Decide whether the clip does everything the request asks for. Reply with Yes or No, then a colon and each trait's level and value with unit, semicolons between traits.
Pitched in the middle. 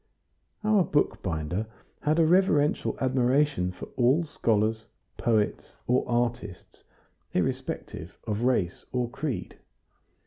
No: low, 125 Hz